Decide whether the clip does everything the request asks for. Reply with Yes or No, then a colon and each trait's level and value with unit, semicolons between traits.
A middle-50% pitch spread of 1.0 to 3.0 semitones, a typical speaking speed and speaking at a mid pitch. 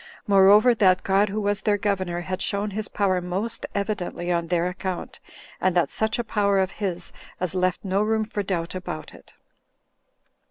No: narrow, 2.4 semitones; average, 175 wpm; high, 195 Hz